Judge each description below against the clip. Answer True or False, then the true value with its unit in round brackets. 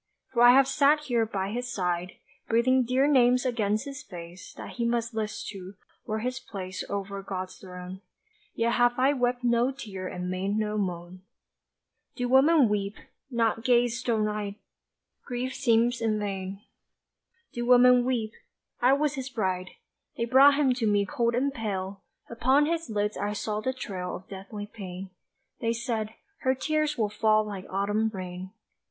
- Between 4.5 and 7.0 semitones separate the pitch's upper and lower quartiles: False (4.1 semitones)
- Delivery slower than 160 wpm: False (165 wpm)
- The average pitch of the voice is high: True (225 Hz)